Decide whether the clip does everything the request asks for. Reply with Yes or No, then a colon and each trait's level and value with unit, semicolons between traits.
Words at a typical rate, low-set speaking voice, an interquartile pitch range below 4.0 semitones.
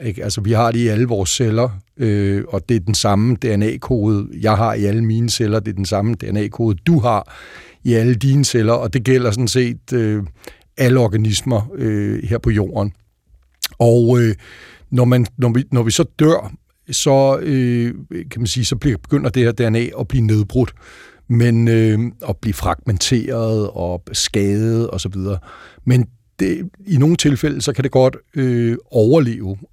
Yes: average, 180 wpm; low, 115 Hz; average, 2.8 semitones